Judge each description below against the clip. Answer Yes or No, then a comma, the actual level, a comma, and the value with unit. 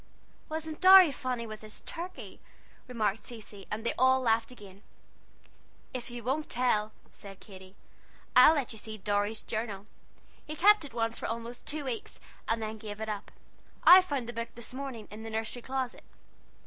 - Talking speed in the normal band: Yes, average, 175 wpm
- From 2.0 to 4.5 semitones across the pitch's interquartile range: Yes, average, 3.3 semitones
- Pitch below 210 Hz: No, high, 230 Hz